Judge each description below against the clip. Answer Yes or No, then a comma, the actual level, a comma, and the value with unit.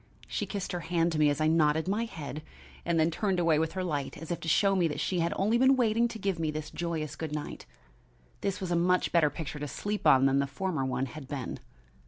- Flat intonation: No, average, 3.7 semitones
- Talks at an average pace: No, fast, 250 wpm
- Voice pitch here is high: No, medium, 165 Hz